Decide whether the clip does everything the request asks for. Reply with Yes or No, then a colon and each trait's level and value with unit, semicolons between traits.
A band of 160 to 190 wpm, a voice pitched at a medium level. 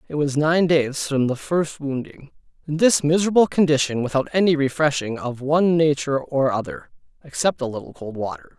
Yes: average, 175 wpm; medium, 150 Hz